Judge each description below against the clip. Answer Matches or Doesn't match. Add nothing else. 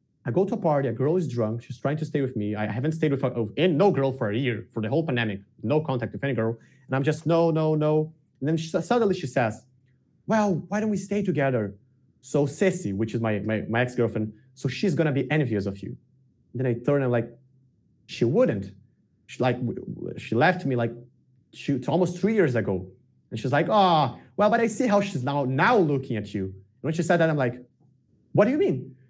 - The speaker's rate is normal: Doesn't match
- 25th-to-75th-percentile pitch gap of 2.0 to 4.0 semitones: Doesn't match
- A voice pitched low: Matches